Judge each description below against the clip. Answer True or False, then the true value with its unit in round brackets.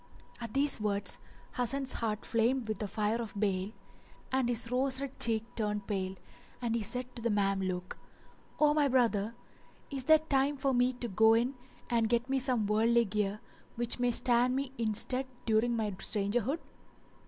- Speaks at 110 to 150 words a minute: False (175 wpm)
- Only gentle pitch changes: False (3.3 semitones)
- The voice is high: True (235 Hz)